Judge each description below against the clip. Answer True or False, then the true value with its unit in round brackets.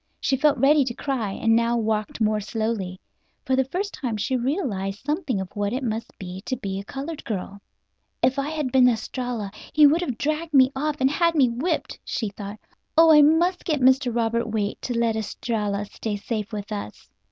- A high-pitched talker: True (240 Hz)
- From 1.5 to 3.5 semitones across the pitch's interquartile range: False (4.9 semitones)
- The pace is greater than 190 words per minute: True (200 wpm)